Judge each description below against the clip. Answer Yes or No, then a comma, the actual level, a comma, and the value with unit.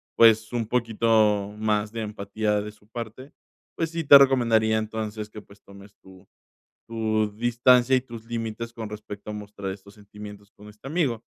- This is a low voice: Yes, low, 110 Hz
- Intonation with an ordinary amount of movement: No, narrow, 2.0 semitones